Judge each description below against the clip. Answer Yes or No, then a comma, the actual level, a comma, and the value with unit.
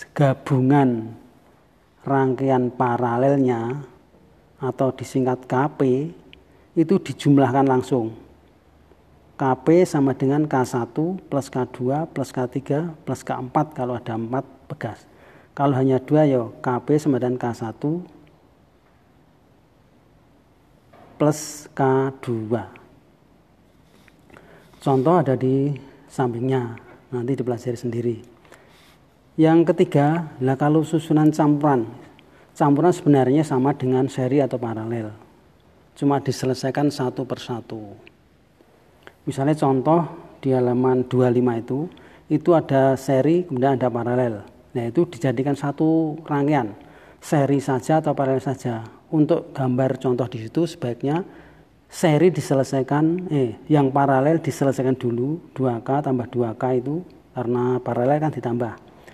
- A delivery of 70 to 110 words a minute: Yes, average, 100 wpm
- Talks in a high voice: No, low, 135 Hz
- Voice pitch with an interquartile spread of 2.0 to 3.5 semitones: Yes, average, 2.8 semitones